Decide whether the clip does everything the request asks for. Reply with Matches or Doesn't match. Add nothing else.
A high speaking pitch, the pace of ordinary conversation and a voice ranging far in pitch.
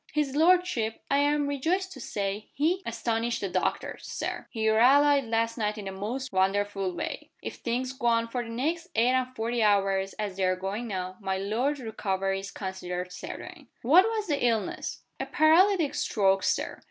Matches